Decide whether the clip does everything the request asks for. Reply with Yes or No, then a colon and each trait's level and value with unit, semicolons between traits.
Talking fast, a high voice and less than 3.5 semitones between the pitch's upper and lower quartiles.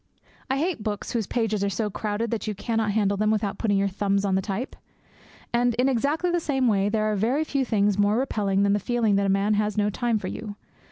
Yes: fast, 240 wpm; high, 215 Hz; average, 3.0 semitones